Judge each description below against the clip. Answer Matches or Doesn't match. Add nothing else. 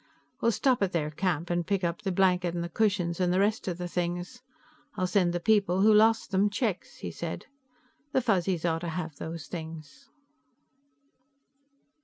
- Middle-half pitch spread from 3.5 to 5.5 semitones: Doesn't match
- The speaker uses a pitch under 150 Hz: Doesn't match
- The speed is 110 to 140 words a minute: Doesn't match